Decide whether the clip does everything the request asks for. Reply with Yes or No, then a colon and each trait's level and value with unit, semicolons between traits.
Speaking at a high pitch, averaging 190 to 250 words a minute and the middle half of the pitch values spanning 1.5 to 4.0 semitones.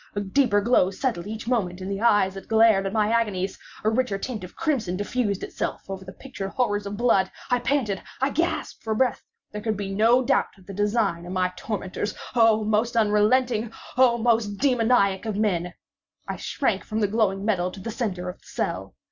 Yes: high, 210 Hz; average, 200 wpm; average, 3.3 semitones